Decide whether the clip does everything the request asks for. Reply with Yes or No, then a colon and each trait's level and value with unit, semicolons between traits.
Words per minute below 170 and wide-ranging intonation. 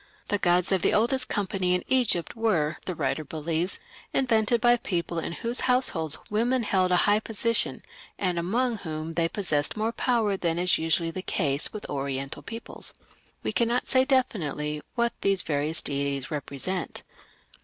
Yes: average, 160 wpm; wide, 6.2 semitones